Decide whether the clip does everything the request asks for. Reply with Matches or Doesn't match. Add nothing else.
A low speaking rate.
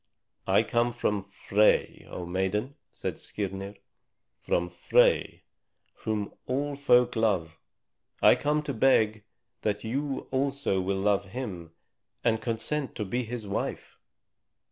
Matches